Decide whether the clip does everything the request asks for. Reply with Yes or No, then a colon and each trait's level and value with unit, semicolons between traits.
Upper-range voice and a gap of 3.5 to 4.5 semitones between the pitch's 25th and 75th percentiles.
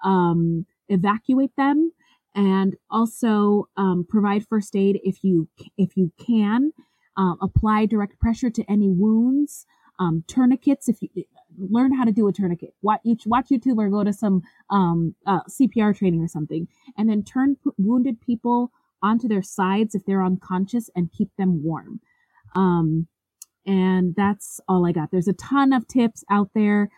Yes: high, 205 Hz; average, 4.2 semitones